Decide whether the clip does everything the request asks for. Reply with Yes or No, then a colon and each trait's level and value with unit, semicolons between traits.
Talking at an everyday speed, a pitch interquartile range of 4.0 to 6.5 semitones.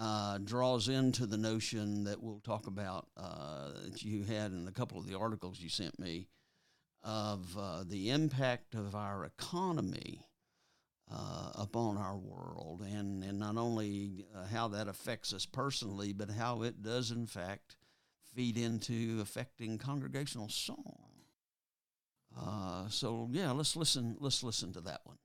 No: average, 150 wpm; average, 3.0 semitones